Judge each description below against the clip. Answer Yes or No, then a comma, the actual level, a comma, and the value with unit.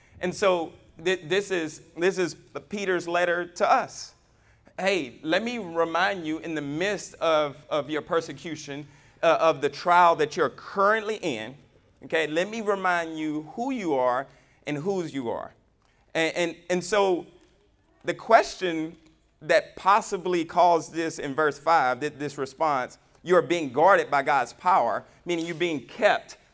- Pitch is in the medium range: Yes, medium, 165 Hz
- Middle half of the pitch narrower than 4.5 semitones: Yes, average, 3.2 semitones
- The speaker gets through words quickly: No, average, 160 wpm